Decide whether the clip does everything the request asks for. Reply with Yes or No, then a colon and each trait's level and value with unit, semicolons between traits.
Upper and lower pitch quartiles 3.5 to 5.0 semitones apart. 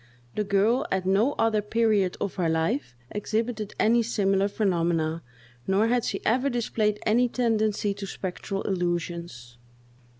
Yes: average, 4.0 semitones